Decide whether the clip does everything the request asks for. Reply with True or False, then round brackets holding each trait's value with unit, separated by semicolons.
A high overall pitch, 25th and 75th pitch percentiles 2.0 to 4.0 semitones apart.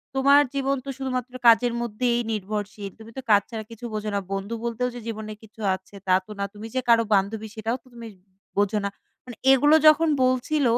True (230 Hz; 3.2 semitones)